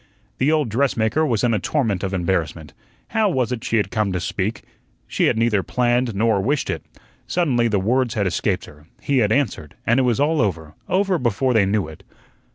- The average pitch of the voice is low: Yes, low, 115 Hz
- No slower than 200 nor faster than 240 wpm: Yes, fast, 205 wpm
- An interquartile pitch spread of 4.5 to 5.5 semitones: Yes, average, 5.0 semitones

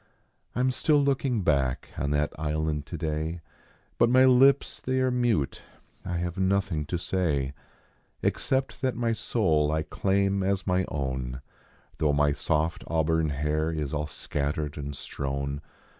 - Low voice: Yes, very low, 80 Hz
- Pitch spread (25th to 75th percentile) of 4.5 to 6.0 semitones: Yes, average, 5.2 semitones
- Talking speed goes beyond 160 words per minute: No, average, 150 wpm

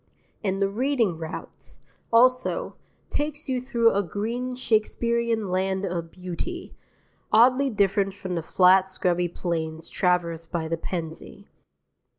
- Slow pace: Yes, slow, 125 wpm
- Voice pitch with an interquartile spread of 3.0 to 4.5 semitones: No, average, 5.0 semitones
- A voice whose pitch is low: No, high, 195 Hz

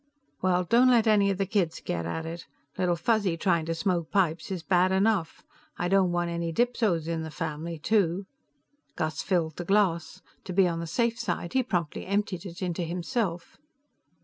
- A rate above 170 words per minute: Yes, average, 185 wpm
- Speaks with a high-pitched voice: No, medium, 180 Hz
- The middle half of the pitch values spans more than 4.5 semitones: No, average, 3.1 semitones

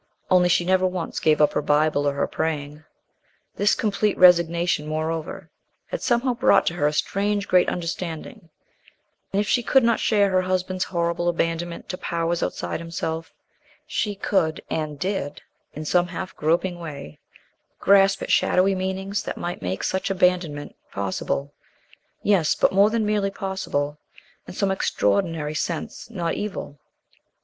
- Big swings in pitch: No, average, 3.6 semitones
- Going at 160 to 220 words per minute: No, average, 150 wpm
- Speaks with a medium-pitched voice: Yes, medium, 175 Hz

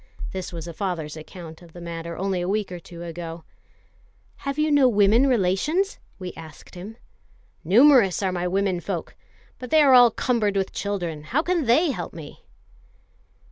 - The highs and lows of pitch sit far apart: Yes, wide, 6.1 semitones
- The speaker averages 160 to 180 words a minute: Yes, average, 170 wpm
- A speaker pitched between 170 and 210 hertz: Yes, high, 190 Hz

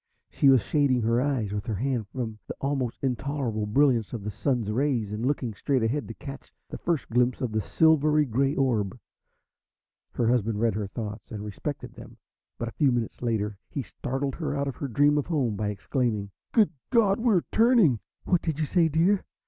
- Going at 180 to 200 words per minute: Yes, average, 195 wpm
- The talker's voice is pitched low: Yes, low, 125 Hz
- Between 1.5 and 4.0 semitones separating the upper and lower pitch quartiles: No, average, 4.7 semitones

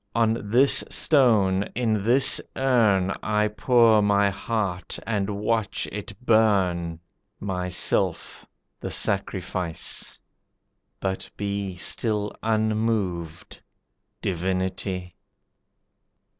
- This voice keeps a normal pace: No, slow, 80 wpm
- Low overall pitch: Yes, low, 100 Hz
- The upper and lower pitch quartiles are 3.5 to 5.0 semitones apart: No, average, 3.0 semitones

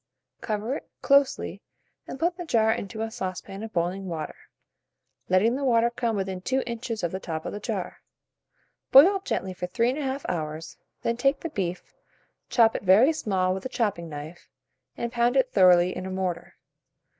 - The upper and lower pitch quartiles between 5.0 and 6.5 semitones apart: Yes, average, 5.3 semitones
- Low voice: No, high, 215 Hz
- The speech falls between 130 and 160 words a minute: No, average, 180 wpm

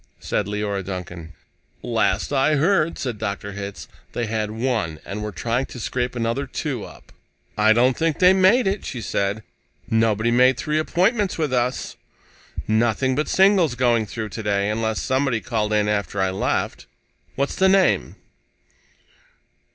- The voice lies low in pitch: Yes, low, 115 Hz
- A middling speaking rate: Yes, average, 150 wpm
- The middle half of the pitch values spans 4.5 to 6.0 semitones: Yes, average, 4.9 semitones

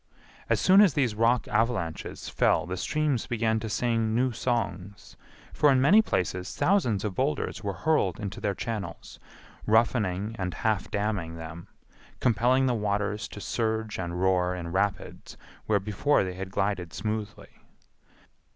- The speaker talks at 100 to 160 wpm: Yes, average, 145 wpm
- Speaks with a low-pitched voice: Yes, low, 105 Hz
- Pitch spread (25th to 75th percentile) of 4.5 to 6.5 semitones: No, average, 4.0 semitones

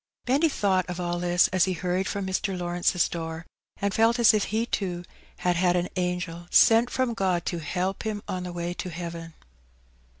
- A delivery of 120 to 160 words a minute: No, average, 200 wpm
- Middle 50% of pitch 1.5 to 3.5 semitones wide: Yes, narrow, 2.5 semitones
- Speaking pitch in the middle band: Yes, medium, 180 Hz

